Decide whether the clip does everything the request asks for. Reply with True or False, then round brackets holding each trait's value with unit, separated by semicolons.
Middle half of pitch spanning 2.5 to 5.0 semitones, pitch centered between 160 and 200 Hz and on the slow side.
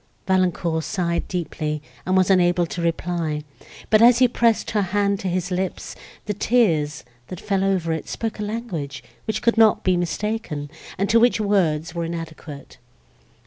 False (4.1 semitones; 185 Hz; 165 wpm)